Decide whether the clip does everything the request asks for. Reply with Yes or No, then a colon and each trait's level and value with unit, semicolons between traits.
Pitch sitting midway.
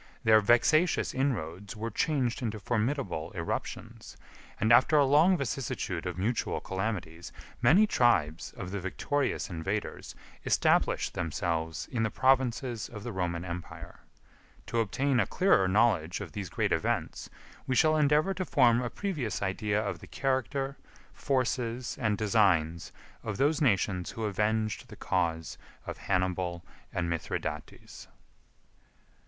No: low, 110 Hz